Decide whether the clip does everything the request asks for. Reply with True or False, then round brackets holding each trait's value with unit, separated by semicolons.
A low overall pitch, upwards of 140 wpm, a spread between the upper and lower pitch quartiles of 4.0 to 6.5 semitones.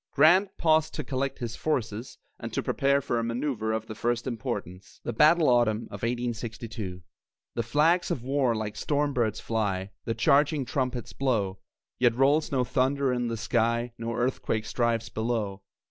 False (120 Hz; 165 wpm; 3.6 semitones)